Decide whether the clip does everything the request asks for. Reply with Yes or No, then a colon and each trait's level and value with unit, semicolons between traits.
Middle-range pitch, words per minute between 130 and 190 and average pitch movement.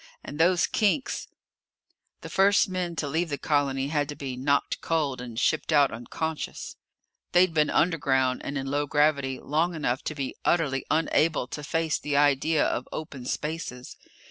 Yes: medium, 150 Hz; average, 165 wpm; average, 3.2 semitones